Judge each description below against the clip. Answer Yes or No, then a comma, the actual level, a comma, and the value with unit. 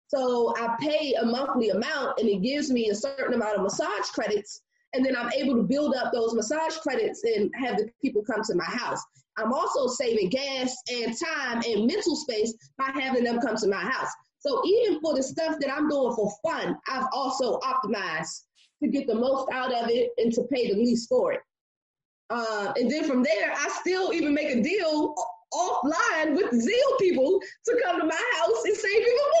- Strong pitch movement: Yes, wide, 5.9 semitones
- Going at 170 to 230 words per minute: Yes, fast, 205 wpm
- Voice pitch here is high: Yes, very high, 270 Hz